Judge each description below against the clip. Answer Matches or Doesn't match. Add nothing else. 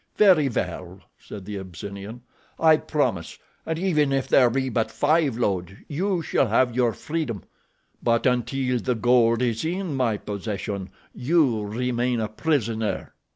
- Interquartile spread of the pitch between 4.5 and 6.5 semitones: Matches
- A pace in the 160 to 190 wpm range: Doesn't match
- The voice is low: Matches